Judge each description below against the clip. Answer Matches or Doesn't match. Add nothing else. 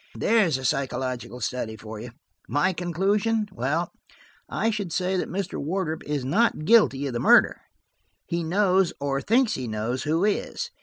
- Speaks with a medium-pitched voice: Matches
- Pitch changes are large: Matches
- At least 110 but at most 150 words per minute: Doesn't match